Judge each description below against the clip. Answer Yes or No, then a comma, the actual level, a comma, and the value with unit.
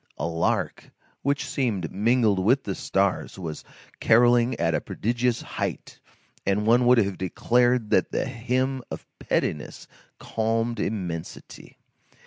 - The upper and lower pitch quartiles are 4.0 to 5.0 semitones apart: Yes, average, 4.3 semitones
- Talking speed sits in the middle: No, slow, 125 wpm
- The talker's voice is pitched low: Yes, low, 115 Hz